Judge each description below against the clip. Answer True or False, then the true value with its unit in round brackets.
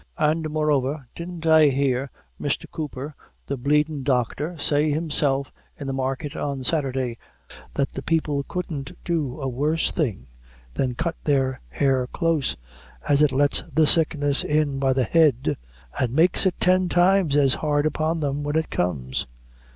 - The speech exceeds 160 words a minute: False (155 wpm)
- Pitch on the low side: False (145 Hz)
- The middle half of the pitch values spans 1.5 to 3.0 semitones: True (2.7 semitones)